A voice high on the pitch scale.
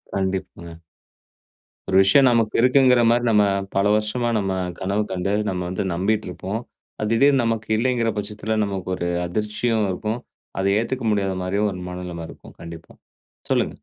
No: low, 105 Hz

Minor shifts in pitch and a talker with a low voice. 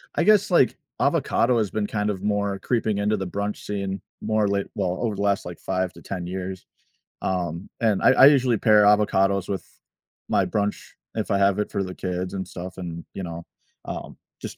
Yes: narrow, 2.1 semitones; low, 100 Hz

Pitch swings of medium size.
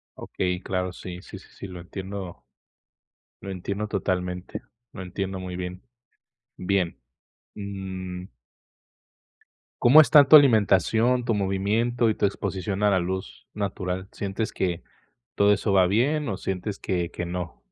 No: narrow, 2.2 semitones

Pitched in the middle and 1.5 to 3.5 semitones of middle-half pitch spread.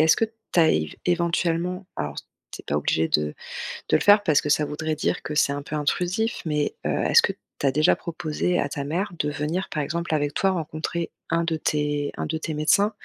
Yes: medium, 155 Hz; average, 2.9 semitones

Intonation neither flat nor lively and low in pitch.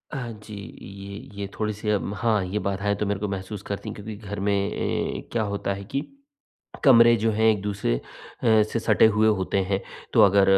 No: narrow, 1.8 semitones; low, 105 Hz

